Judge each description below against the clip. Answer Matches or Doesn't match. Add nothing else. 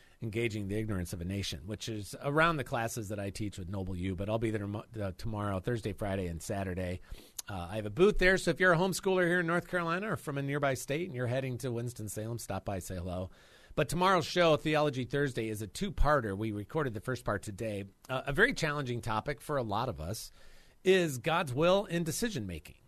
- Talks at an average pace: Doesn't match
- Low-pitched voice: Matches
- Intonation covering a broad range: Matches